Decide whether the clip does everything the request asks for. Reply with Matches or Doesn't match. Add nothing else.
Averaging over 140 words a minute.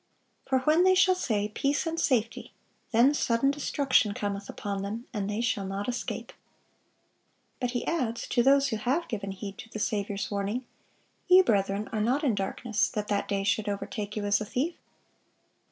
Matches